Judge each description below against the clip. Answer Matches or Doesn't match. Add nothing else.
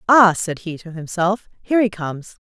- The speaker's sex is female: Matches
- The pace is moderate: Matches